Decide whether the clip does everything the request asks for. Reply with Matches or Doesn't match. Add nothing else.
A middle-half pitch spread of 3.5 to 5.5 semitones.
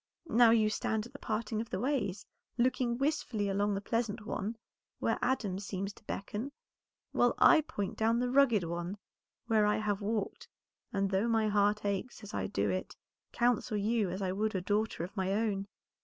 Doesn't match